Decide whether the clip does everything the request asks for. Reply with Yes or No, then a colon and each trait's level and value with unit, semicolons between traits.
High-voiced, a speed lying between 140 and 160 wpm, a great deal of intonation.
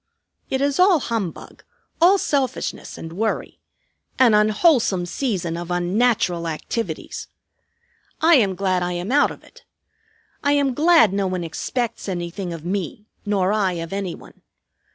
Yes: high, 200 Hz; average, 145 wpm; wide, 6.5 semitones